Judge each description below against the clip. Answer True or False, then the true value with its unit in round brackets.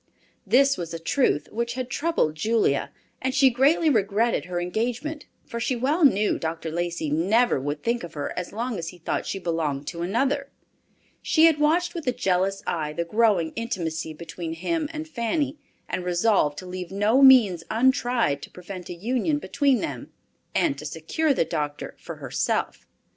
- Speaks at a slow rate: False (175 wpm)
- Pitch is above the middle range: True (210 Hz)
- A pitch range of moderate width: False (7.7 semitones)